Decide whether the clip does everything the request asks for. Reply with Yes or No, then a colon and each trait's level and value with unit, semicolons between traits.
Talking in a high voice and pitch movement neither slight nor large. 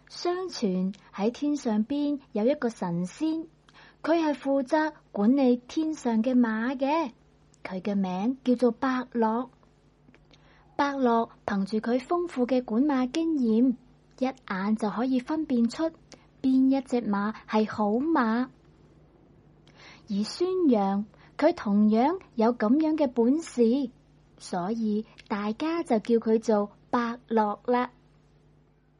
Yes: high, 240 Hz; average, 4.6 semitones